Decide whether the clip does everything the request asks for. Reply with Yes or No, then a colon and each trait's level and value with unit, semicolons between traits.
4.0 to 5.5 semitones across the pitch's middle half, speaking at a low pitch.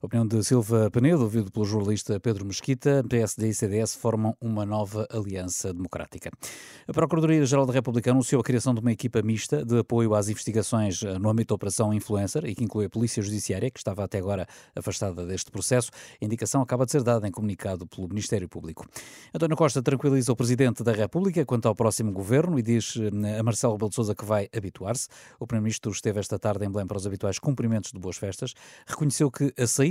No: average, 3.2 semitones; low, 110 Hz